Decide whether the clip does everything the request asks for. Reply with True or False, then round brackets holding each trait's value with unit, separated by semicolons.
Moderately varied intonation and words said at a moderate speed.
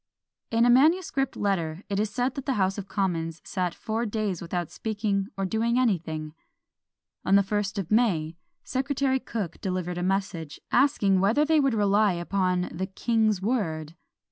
True (4.4 semitones; 165 wpm)